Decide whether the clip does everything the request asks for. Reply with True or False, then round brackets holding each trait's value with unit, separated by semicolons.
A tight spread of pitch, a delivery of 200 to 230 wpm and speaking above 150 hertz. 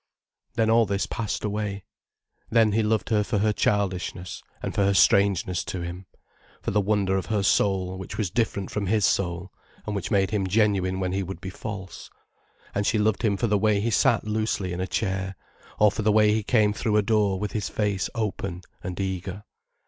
False (2.1 semitones; 205 wpm; 100 Hz)